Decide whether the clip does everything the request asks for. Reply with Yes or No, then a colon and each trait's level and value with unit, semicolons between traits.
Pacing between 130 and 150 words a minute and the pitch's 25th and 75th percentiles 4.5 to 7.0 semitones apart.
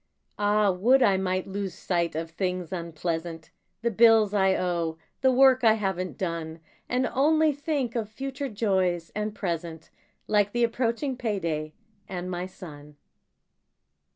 Yes: average, 140 wpm; average, 5.3 semitones